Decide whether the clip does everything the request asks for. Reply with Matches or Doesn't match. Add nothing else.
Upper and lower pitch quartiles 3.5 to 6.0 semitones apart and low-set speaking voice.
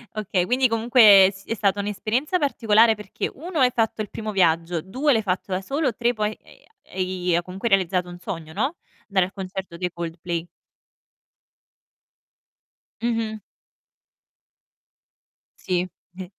Doesn't match